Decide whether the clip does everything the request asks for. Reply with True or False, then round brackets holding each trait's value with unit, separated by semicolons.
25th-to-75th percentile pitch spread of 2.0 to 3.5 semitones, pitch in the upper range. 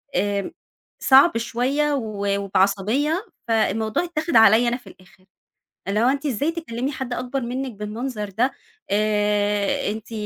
False (4.5 semitones; 230 Hz)